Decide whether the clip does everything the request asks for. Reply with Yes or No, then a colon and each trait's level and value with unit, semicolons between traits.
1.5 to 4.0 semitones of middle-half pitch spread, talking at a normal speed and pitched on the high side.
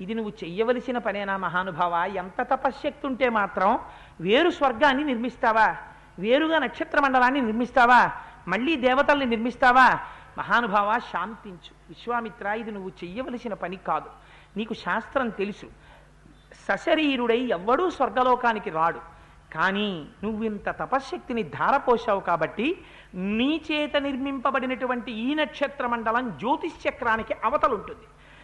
No: average, 5.2 semitones; average, 105 wpm; high, 240 Hz